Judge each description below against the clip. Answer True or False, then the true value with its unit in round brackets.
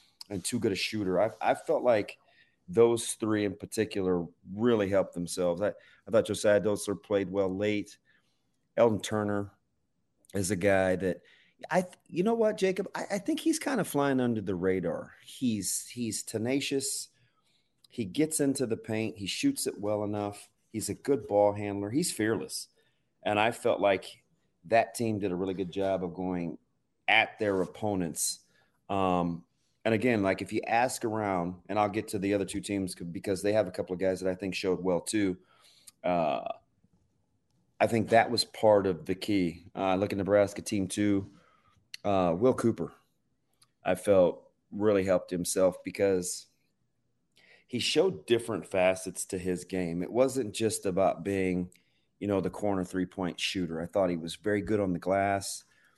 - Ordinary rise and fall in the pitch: True (3.2 semitones)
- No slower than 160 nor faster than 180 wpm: True (175 wpm)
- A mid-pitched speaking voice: False (100 Hz)